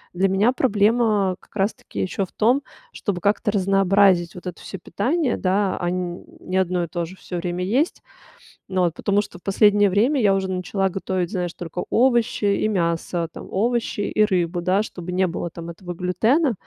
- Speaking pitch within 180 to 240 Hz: Yes, high, 190 Hz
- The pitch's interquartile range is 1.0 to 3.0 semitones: Yes, average, 2.7 semitones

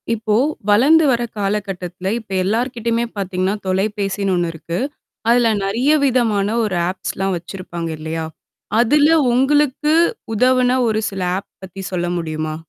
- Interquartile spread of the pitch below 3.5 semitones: No, average, 4.5 semitones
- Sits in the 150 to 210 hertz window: Yes, high, 205 Hz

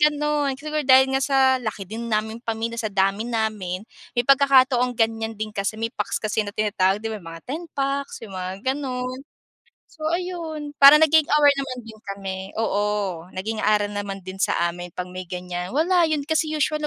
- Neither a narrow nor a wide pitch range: No, wide, 5.8 semitones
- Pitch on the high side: Yes, high, 225 Hz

